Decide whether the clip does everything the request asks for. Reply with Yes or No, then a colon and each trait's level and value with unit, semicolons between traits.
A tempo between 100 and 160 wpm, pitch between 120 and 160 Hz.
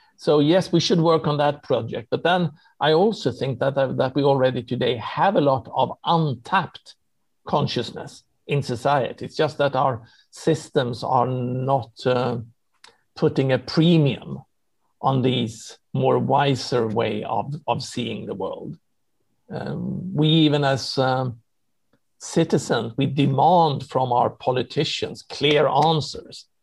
Yes: slow, 135 wpm; low, 135 Hz